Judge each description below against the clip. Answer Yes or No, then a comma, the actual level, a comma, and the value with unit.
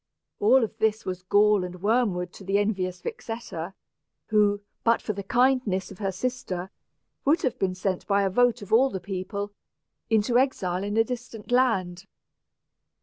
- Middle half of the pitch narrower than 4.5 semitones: Yes, average, 3.8 semitones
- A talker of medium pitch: No, high, 205 Hz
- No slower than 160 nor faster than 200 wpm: Yes, average, 170 wpm